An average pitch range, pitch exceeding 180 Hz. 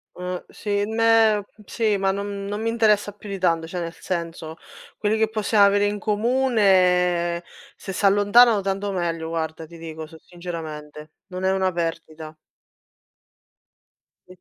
Yes: average, 3.6 semitones; high, 190 Hz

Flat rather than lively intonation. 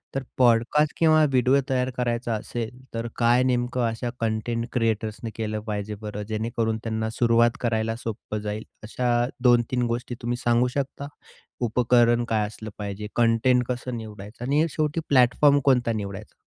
Yes: narrow, 2.1 semitones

